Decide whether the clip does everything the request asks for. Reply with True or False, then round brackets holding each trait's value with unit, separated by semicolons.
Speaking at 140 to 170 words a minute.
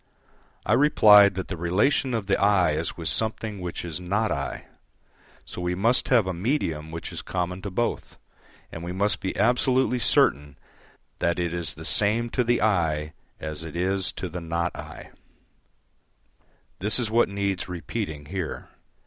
True (165 wpm)